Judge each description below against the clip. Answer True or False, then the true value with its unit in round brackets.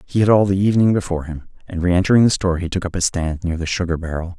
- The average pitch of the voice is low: True (90 Hz)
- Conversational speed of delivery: False (275 wpm)